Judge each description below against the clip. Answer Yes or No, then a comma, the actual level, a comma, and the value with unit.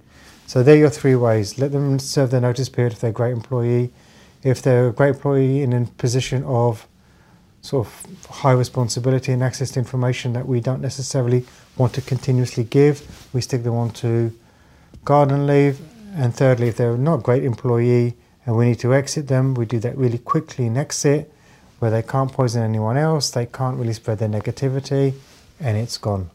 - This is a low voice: Yes, low, 125 Hz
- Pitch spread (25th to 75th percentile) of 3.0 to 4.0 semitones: No, narrow, 2.4 semitones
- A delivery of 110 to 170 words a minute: No, average, 195 wpm